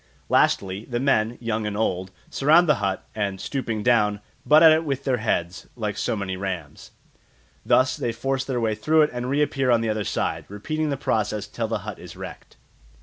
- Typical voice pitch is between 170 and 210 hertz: No, low, 115 Hz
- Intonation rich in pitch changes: No, average, 4.7 semitones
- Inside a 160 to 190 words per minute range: No, average, 200 wpm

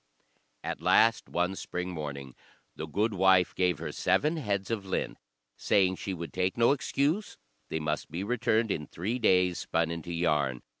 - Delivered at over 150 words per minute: Yes, average, 160 wpm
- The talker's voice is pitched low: Yes, very low, 90 Hz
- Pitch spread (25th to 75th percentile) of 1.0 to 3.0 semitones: No, average, 4.8 semitones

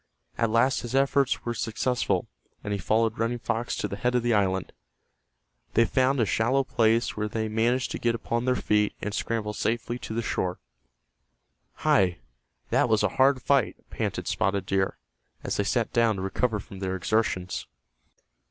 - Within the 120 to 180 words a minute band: Yes, average, 175 wpm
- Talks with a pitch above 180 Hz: No, low, 115 Hz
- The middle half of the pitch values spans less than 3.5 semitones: Yes, average, 2.7 semitones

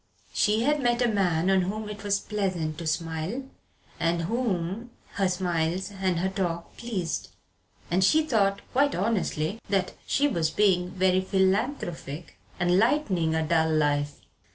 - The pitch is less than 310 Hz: Yes, high, 190 Hz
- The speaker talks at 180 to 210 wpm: No, average, 150 wpm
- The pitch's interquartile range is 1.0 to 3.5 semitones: No, average, 3.9 semitones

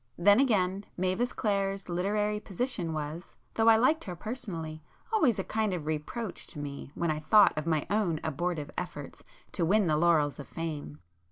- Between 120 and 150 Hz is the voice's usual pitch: No, medium, 180 Hz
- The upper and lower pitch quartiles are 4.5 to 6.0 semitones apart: Yes, average, 5.1 semitones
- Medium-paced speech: Yes, average, 175 wpm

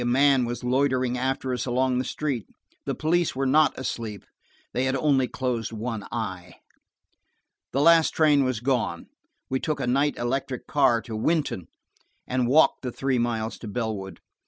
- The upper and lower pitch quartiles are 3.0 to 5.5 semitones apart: No, narrow, 2.6 semitones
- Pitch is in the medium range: No, low, 130 Hz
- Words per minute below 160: No, average, 165 wpm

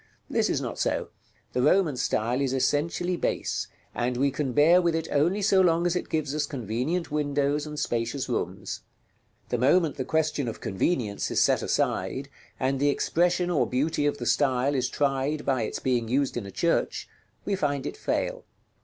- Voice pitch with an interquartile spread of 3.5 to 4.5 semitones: Yes, average, 4.1 semitones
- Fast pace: No, average, 185 wpm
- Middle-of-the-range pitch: Yes, medium, 145 Hz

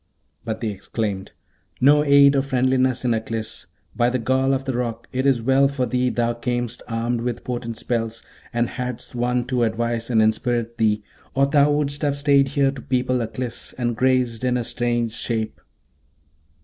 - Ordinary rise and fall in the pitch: No, narrow, 2.2 semitones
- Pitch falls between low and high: No, low, 125 Hz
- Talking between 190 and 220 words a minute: No, average, 175 wpm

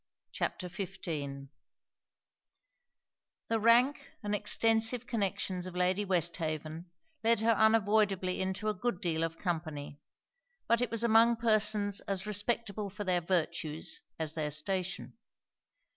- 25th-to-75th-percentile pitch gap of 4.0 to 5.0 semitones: Yes, average, 4.3 semitones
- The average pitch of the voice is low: No, high, 195 Hz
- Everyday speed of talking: No, slow, 125 wpm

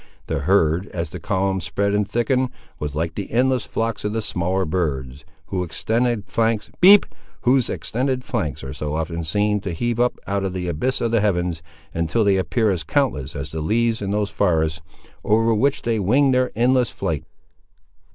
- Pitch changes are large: Yes, wide, 5.8 semitones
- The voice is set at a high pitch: No, low, 100 Hz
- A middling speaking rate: Yes, average, 170 wpm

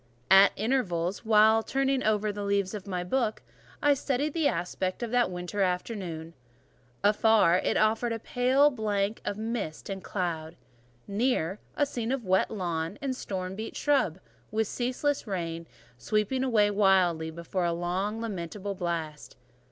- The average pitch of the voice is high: Yes, high, 205 Hz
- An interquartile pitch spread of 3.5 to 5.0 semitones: Yes, average, 4.4 semitones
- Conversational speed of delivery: Yes, average, 150 wpm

